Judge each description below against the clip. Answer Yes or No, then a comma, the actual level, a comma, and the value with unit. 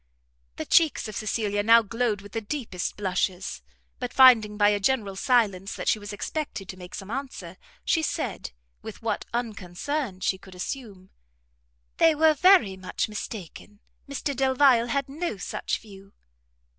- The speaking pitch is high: Yes, high, 215 Hz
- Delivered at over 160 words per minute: No, average, 155 wpm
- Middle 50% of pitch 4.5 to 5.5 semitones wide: Yes, average, 5.2 semitones